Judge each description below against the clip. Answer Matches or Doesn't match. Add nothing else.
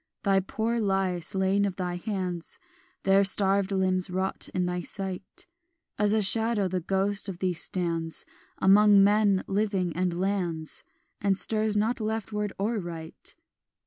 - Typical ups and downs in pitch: Doesn't match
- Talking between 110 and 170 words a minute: Matches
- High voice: Matches